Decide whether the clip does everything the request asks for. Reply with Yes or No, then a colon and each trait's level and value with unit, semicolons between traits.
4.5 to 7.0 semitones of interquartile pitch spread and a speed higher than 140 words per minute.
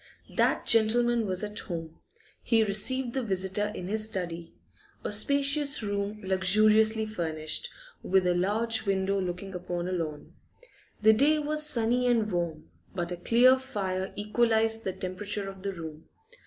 No: average, 3.7 semitones; average, 150 wpm